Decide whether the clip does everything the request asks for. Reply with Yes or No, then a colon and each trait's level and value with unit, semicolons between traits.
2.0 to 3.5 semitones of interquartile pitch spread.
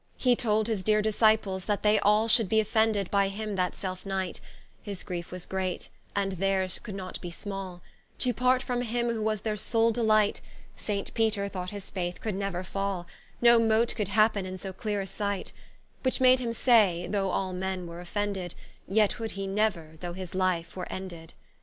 Yes: average, 2.8 semitones